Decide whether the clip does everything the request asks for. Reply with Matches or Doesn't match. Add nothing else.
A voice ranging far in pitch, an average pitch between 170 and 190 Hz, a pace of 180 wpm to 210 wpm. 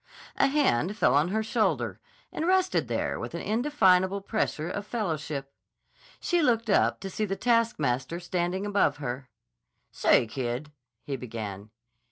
Doesn't match